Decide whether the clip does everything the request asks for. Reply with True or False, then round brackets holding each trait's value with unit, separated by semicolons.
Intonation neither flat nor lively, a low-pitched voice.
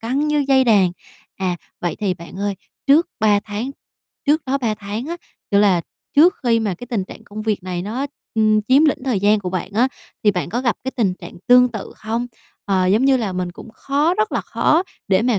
False (4.9 semitones; 220 Hz)